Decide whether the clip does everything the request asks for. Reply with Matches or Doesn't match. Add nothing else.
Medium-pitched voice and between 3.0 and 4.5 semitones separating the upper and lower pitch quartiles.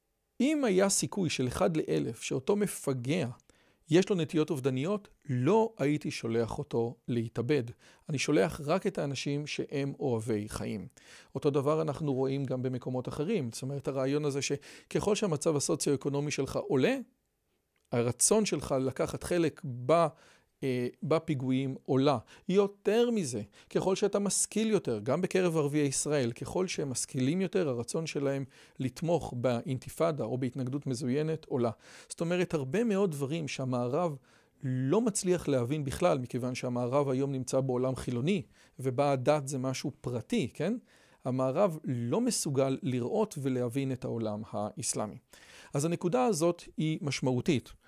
Doesn't match